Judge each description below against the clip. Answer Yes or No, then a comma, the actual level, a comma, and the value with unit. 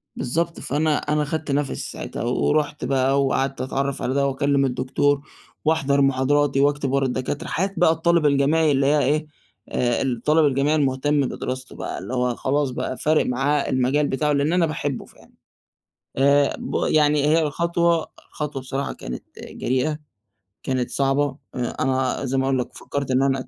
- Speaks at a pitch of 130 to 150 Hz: Yes, medium, 140 Hz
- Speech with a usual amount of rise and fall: No, narrow, 2.1 semitones